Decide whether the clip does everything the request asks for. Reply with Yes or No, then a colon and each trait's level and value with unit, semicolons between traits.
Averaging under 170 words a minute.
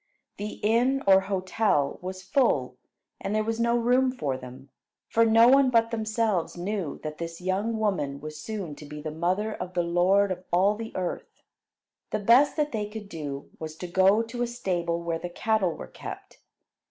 No: average, 190 wpm